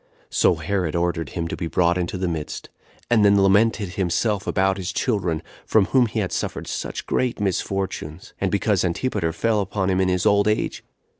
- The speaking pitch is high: No, very low, 95 Hz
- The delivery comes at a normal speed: Yes, average, 190 wpm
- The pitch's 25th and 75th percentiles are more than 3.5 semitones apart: No, average, 3.0 semitones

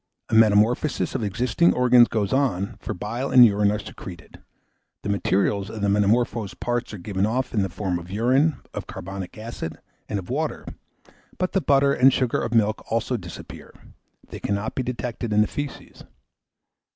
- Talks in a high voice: No, low, 110 Hz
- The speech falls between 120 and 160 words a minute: No, average, 175 wpm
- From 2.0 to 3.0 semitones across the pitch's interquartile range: No, average, 3.8 semitones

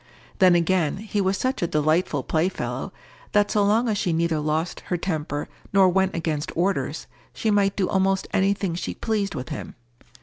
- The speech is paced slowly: No, average, 180 wpm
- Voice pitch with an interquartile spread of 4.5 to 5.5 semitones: No, average, 3.6 semitones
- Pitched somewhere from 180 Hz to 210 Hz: Yes, medium, 185 Hz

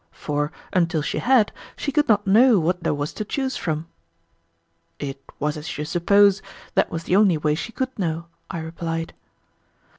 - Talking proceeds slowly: No, average, 175 wpm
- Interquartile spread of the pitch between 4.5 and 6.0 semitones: Yes, average, 5.2 semitones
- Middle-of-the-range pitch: Yes, medium, 170 Hz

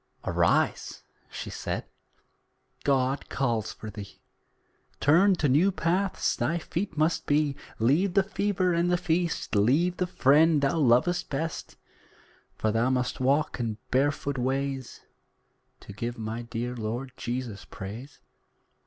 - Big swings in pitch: Yes, wide, 5.8 semitones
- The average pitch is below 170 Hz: Yes, medium, 140 Hz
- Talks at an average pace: No, slow, 130 wpm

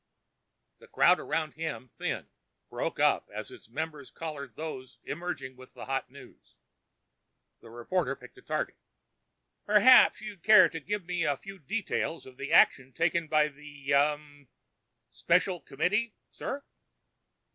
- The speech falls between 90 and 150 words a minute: Yes, average, 140 wpm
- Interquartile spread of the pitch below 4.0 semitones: No, average, 4.8 semitones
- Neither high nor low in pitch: Yes, medium, 155 Hz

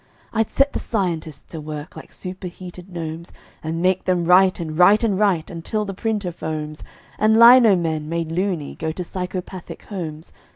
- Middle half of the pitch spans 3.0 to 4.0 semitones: Yes, average, 3.4 semitones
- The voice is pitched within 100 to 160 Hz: No, medium, 180 Hz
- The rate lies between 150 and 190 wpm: Yes, average, 170 wpm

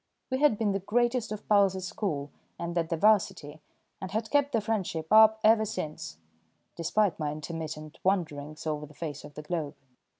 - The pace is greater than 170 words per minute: Yes, average, 180 wpm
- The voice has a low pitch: No, medium, 180 Hz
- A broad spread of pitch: Yes, wide, 5.9 semitones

